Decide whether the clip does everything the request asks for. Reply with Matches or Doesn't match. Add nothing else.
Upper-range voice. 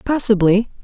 Matches